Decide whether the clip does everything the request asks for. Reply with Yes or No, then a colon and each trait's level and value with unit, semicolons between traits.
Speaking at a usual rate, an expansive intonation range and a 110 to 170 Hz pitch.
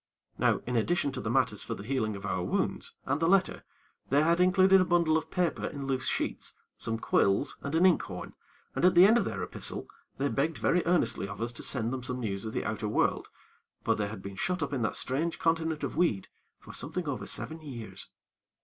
No: fast, 220 wpm; wide, 7.0 semitones; medium, 140 Hz